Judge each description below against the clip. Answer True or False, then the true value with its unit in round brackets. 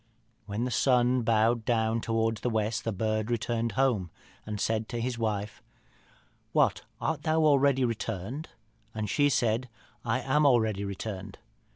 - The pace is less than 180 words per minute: True (150 wpm)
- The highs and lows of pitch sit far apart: False (2.6 semitones)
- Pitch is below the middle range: True (115 Hz)